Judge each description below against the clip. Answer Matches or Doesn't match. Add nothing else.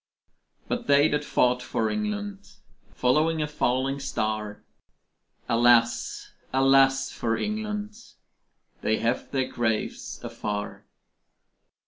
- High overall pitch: Doesn't match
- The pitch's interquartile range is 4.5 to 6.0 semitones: Matches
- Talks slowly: Matches